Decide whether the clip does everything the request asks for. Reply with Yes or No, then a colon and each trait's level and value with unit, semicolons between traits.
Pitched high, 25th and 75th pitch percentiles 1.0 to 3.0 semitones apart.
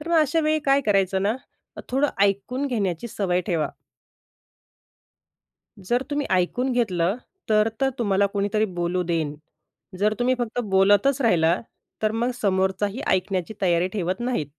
No: high, 205 Hz; average, 5.0 semitones